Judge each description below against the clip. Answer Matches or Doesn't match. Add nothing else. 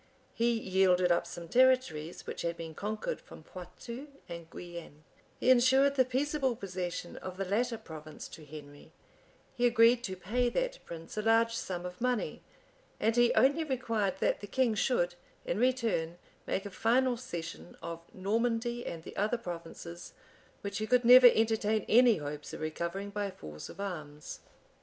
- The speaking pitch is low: Doesn't match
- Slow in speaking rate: Doesn't match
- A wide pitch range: Matches